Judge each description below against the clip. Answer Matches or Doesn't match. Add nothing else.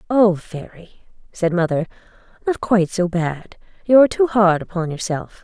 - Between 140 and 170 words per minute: Matches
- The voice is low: Doesn't match